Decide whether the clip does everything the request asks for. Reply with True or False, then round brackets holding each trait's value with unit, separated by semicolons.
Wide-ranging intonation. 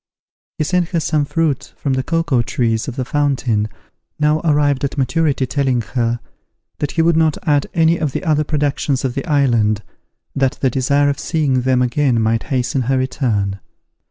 False (3.2 semitones)